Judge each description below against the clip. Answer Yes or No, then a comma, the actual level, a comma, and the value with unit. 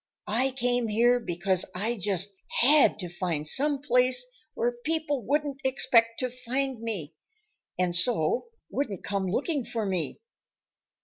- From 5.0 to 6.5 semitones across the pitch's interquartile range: Yes, wide, 5.5 semitones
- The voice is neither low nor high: No, high, 235 Hz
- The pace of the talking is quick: No, slow, 135 wpm